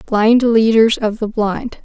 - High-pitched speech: Yes, high, 220 Hz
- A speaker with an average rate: Yes, average, 165 wpm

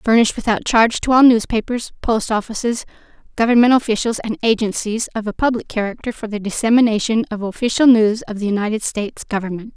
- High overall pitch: Yes, high, 225 Hz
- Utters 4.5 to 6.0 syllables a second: No, 6.2 syllables/s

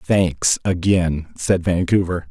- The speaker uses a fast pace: No, slow, 105 wpm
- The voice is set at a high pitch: No, very low, 90 Hz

